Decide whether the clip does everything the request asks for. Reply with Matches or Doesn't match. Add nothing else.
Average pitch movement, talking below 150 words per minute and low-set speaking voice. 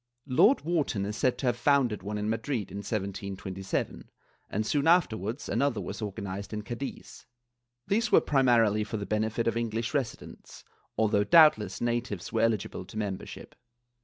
Doesn't match